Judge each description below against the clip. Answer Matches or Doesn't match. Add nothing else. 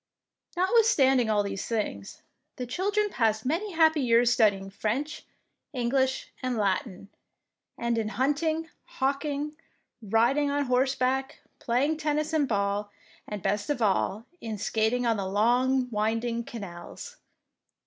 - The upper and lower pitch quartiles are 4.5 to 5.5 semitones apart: Matches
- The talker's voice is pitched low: Doesn't match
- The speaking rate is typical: Doesn't match